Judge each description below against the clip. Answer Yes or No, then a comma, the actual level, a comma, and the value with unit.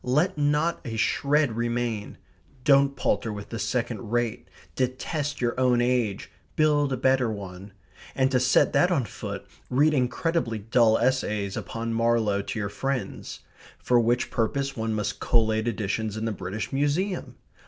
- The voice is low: Yes, low, 120 Hz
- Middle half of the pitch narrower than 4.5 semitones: Yes, average, 3.7 semitones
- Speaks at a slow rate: No, average, 155 wpm